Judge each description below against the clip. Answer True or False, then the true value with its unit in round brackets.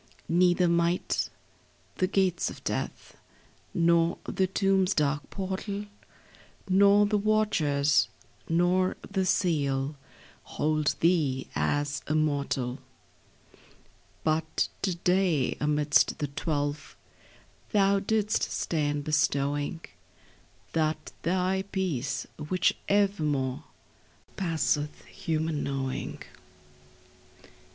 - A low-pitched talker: False (165 Hz)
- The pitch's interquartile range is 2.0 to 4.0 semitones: False (4.4 semitones)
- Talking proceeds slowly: True (85 wpm)